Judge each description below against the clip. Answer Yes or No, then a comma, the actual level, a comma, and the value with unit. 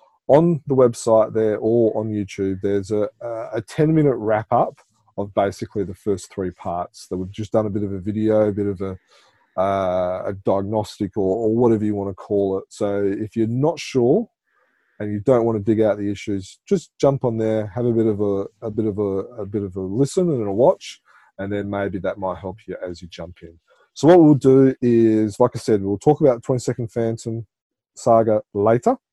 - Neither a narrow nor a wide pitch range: Yes, average, 3.0 semitones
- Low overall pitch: Yes, low, 110 Hz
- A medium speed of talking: No, fast, 220 wpm